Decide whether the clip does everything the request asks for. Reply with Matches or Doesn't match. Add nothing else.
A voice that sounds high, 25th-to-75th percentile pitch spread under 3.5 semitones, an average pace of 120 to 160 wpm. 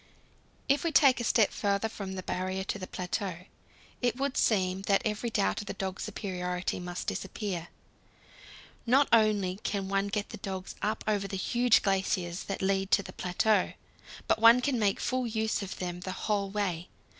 Doesn't match